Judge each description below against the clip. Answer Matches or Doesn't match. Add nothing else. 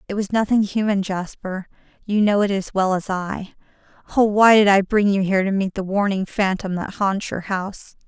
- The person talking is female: Matches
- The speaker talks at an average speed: Doesn't match